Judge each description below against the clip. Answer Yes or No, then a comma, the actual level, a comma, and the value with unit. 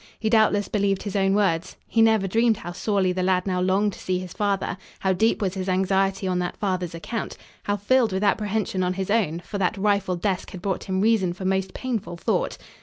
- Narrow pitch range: Yes, narrow, 2.1 semitones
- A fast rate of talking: Yes, fast, 220 wpm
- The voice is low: No, high, 195 Hz